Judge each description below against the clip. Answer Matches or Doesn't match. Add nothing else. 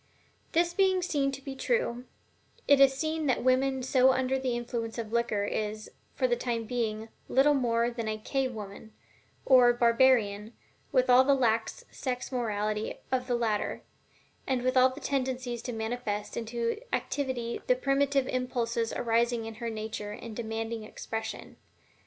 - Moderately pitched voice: Doesn't match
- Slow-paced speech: Doesn't match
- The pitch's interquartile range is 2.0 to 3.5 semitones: Matches